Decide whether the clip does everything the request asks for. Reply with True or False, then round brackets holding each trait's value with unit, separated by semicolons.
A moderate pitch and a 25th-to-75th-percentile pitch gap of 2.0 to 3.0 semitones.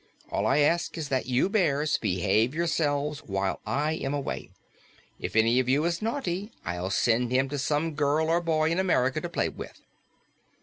False (145 Hz; 4.5 semitones)